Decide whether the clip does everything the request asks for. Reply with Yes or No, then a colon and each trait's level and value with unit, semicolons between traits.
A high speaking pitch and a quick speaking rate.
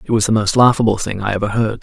No: low, 110 Hz; fast, 295 wpm